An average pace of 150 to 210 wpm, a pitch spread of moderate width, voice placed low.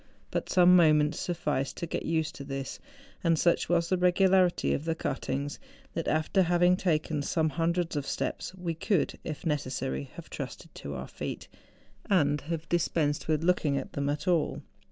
No: average, 175 wpm; average, 3.2 semitones; medium, 160 Hz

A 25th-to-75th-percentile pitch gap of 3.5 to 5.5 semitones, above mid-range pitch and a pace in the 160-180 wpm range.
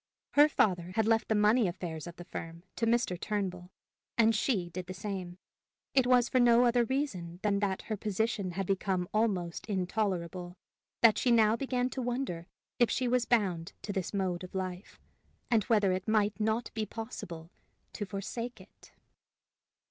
Yes: average, 4.1 semitones; high, 205 Hz; average, 170 wpm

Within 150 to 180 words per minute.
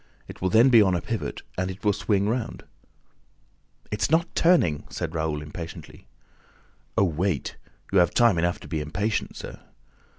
Yes: average, 160 wpm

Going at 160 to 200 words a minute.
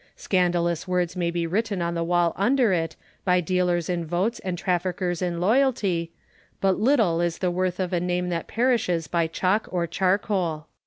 Yes: average, 175 wpm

